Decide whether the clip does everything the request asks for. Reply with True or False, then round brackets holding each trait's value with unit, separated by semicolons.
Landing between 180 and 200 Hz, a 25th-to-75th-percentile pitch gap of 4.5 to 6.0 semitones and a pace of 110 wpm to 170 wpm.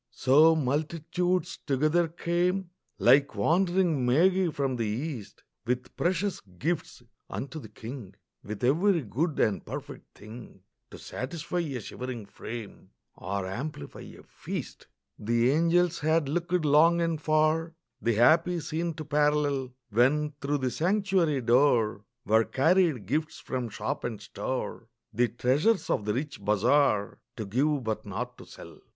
False (145 Hz; 5.5 semitones; 140 wpm)